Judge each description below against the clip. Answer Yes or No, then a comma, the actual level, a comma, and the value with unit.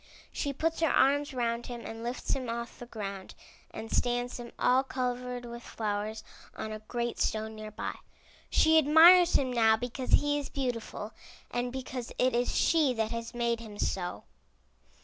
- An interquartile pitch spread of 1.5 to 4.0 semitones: Yes, average, 2.8 semitones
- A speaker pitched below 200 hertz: No, high, 240 Hz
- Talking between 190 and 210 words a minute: No, average, 170 wpm